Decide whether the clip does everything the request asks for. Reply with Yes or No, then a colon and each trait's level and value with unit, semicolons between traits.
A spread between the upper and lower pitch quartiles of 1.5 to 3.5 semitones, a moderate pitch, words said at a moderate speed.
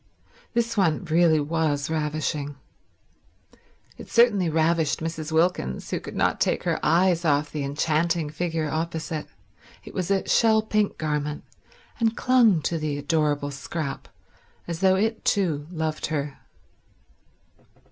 No: average, 3.2 semitones; medium, 160 Hz; slow, 130 wpm